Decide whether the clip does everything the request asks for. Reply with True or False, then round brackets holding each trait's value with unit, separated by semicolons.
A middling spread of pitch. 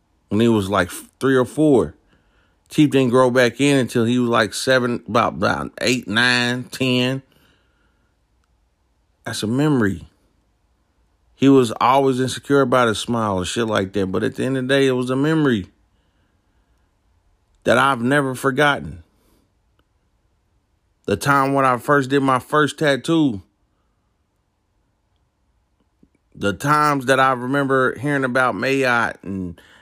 False (5.8 semitones)